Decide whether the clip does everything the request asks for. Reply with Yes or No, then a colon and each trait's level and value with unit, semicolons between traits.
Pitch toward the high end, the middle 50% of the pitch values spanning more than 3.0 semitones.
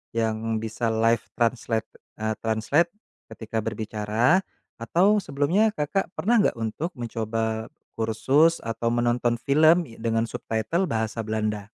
No: low, 115 Hz; average, 4.8 semitones